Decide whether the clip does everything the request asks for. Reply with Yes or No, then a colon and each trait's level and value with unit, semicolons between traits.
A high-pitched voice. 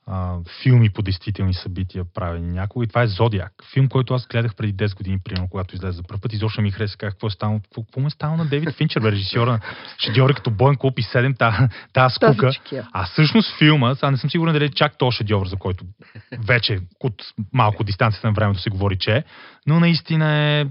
No: low, 115 Hz